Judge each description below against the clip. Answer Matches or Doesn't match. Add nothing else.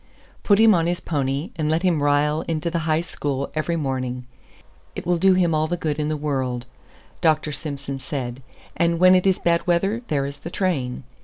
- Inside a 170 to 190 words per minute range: Doesn't match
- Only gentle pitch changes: Doesn't match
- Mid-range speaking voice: Matches